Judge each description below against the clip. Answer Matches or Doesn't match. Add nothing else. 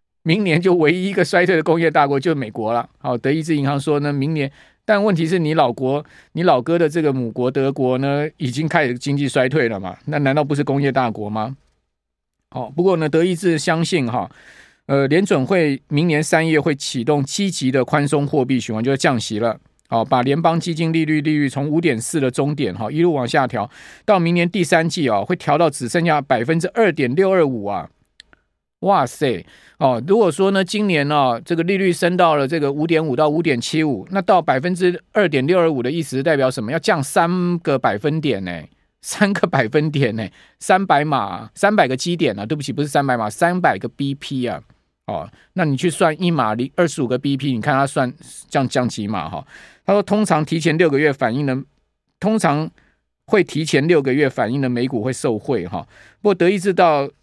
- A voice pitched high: Doesn't match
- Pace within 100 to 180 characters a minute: Doesn't match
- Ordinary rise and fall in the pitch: Matches